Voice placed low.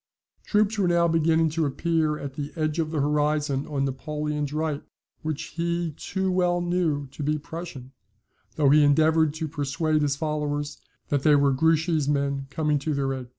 No: medium, 150 Hz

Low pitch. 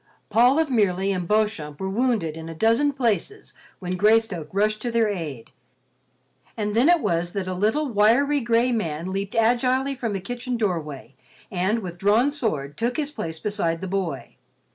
No: high, 210 Hz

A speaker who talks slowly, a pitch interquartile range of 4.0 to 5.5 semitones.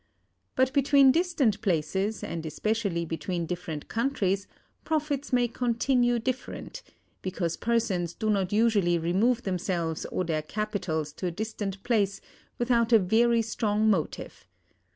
Yes: slow, 130 wpm; average, 5.2 semitones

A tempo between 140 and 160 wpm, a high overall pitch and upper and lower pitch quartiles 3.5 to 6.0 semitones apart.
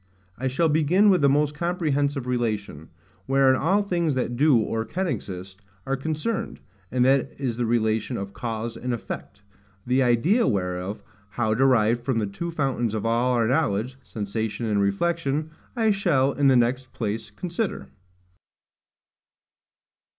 No: average, 150 wpm; low, 125 Hz; average, 5.1 semitones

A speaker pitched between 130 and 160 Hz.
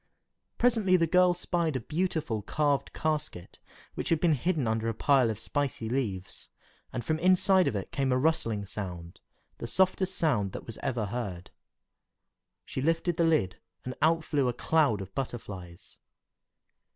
Yes: medium, 140 Hz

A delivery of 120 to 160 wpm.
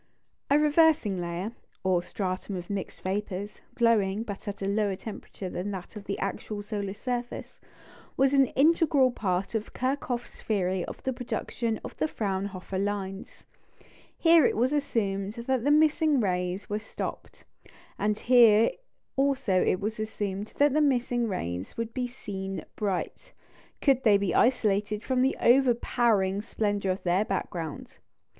Yes: average, 150 wpm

